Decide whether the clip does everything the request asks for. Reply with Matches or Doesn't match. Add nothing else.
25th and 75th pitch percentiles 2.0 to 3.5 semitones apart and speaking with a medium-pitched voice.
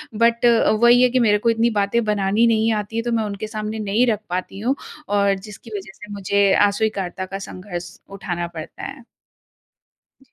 Doesn't match